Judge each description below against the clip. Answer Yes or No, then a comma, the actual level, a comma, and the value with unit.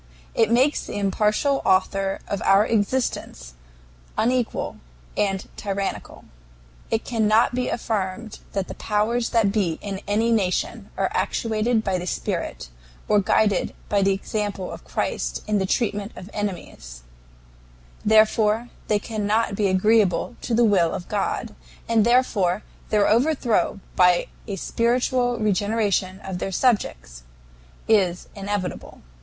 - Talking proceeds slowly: Yes, slow, 130 wpm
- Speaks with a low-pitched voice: No, high, 210 Hz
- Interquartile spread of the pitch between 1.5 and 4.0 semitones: Yes, average, 2.8 semitones